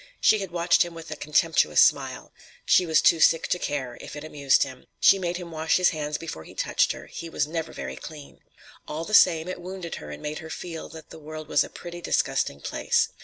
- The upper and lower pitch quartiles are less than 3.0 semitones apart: Yes, narrow, 2.5 semitones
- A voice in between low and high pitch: Yes, medium, 160 Hz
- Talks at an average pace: No, fast, 225 wpm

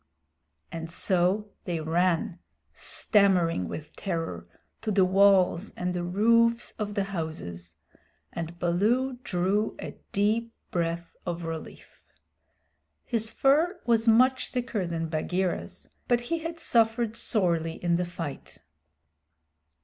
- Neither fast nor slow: No, slow, 120 wpm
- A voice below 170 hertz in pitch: No, high, 190 Hz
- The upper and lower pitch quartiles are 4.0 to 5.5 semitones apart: Yes, average, 5.0 semitones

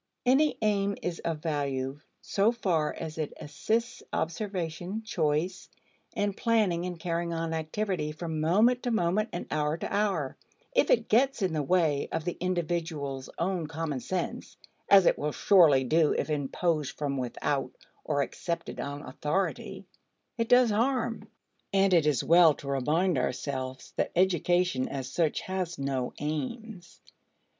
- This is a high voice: No, medium, 170 Hz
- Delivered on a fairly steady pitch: No, average, 4.6 semitones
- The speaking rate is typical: Yes, average, 150 wpm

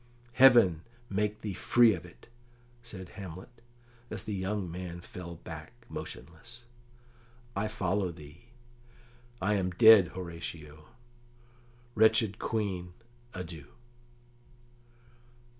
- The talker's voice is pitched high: No, very low, 95 Hz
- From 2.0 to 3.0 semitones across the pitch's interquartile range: No, average, 3.8 semitones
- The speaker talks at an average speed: No, slow, 95 wpm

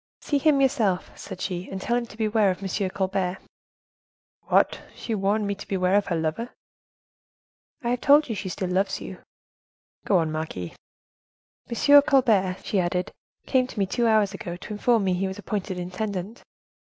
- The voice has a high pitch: Yes, high, 200 Hz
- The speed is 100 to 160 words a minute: No, average, 180 wpm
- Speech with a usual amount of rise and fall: Yes, average, 3.8 semitones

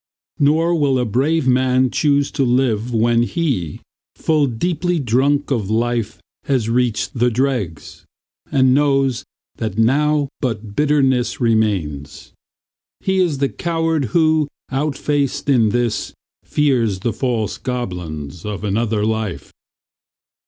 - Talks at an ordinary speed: No, slow, 120 wpm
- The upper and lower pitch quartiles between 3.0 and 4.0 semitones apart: No, average, 4.5 semitones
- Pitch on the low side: Yes, low, 125 Hz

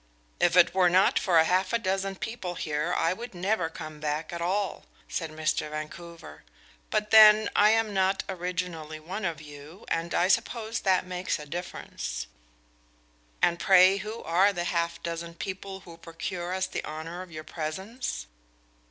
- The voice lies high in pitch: No, medium, 180 Hz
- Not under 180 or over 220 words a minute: No, average, 165 wpm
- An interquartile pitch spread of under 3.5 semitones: Yes, average, 2.7 semitones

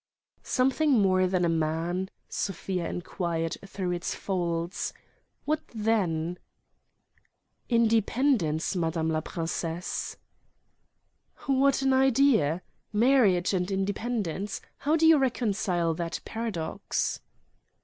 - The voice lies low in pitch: No, high, 190 Hz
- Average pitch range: No, wide, 6.0 semitones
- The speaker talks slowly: Yes, slow, 95 wpm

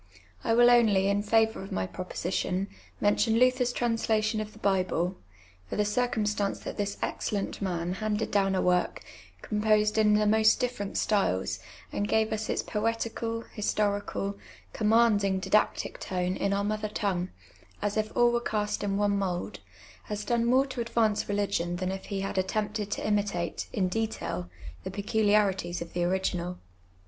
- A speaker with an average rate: Yes, average, 165 wpm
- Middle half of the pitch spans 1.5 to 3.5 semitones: Yes, narrow, 2.4 semitones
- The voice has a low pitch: No, high, 210 Hz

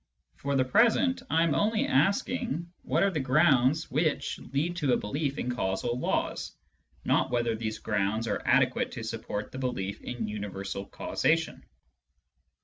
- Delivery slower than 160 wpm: Yes, average, 150 wpm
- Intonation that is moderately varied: No, wide, 6.6 semitones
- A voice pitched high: No, low, 130 Hz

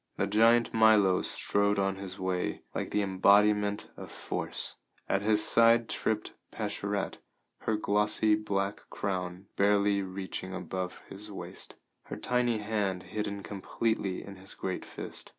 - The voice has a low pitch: Yes, low, 100 Hz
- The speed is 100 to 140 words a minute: Yes, slow, 135 wpm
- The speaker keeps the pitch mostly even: Yes, narrow, 1.8 semitones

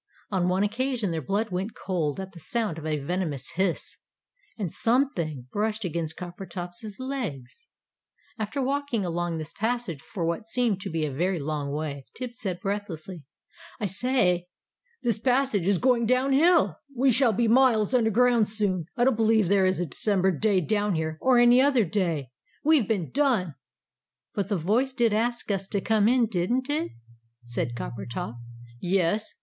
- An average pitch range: No, wide, 5.7 semitones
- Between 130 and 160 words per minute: No, average, 170 wpm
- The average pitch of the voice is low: No, high, 205 Hz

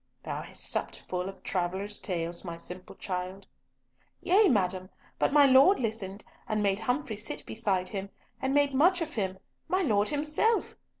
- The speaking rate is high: No, average, 160 wpm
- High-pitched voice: Yes, high, 210 Hz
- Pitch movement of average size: No, wide, 7.2 semitones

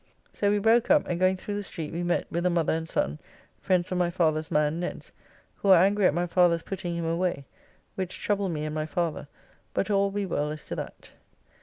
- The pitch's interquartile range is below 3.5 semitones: Yes, average, 3.1 semitones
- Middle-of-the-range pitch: Yes, medium, 175 Hz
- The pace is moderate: No, fast, 230 wpm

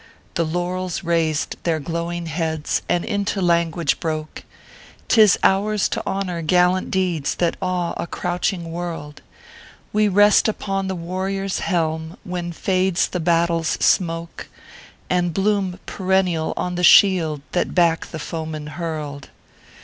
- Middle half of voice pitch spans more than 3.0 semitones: No, narrow, 2.4 semitones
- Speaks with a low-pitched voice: No, medium, 175 Hz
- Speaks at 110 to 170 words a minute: Yes, average, 140 wpm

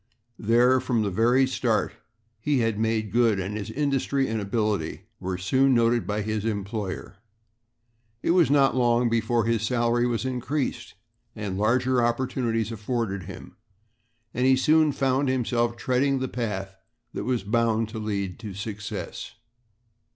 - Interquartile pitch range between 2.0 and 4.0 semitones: Yes, average, 3.2 semitones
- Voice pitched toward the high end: No, low, 115 Hz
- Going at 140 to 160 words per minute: Yes, average, 145 wpm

